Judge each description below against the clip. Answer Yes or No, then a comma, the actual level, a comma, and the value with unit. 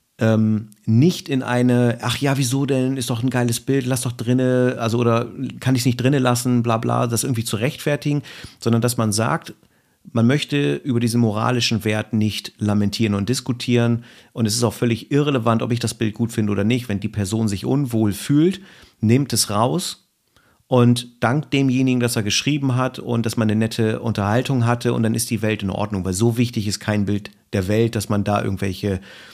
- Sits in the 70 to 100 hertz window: No, low, 120 Hz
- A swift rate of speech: Yes, fast, 200 wpm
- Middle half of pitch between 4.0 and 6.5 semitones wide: No, average, 2.8 semitones